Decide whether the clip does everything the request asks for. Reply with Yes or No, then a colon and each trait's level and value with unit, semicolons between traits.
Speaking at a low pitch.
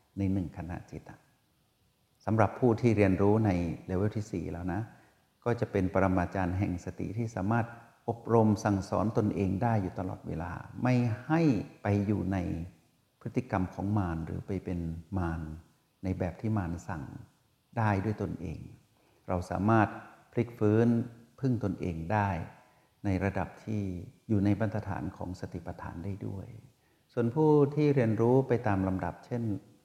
Yes: low, 105 Hz